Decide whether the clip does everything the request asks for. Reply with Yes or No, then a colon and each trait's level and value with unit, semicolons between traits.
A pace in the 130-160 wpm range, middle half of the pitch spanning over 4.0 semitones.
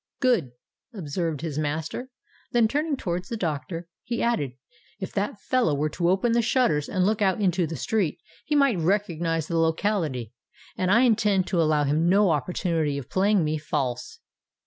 No: average, 170 wpm; wide, 5.4 semitones